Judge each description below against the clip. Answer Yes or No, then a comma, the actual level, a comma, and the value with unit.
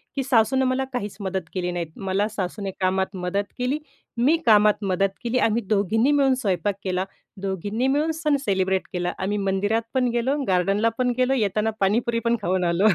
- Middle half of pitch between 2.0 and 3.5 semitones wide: No, average, 4.6 semitones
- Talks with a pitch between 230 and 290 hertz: No, high, 210 Hz